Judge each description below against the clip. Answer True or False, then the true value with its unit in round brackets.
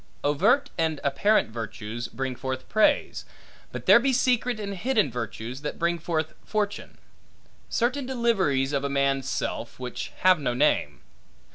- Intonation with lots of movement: True (8.4 semitones)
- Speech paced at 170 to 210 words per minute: False (145 wpm)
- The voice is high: False (155 Hz)